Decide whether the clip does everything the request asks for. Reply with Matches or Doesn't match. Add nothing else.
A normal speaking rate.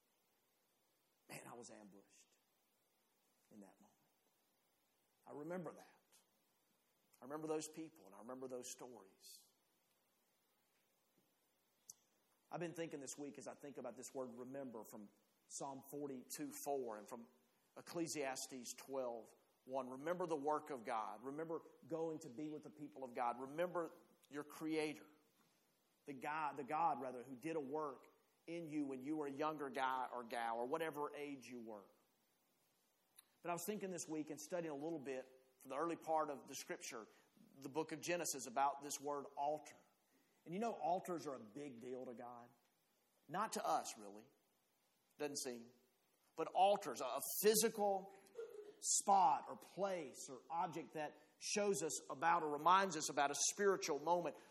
Matches